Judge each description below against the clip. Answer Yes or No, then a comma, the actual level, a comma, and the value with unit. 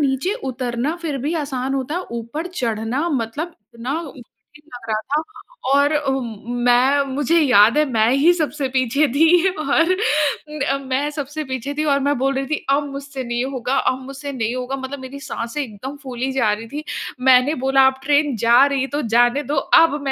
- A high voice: Yes, very high, 270 Hz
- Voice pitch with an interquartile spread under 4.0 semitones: Yes, average, 2.9 semitones